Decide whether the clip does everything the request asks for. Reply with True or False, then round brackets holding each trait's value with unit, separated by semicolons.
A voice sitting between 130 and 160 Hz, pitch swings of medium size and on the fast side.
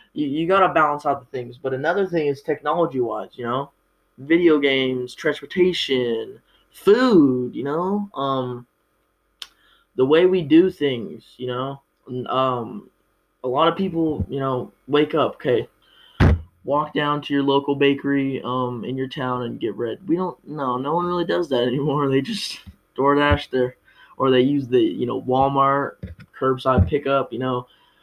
False (140 Hz; 3.3 semitones; 165 wpm)